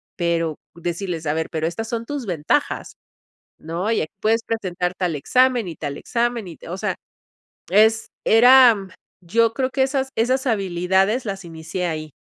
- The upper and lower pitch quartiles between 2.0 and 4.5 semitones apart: No, wide, 5.4 semitones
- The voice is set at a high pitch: Yes, high, 195 Hz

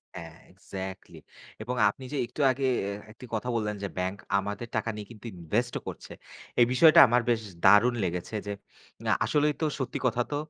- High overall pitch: No, low, 110 Hz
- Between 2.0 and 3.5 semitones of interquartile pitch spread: No, average, 4.4 semitones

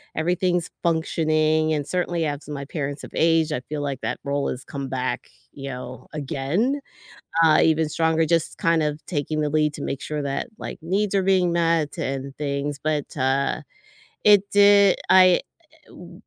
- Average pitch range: Yes, average, 3.3 semitones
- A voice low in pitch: No, medium, 155 Hz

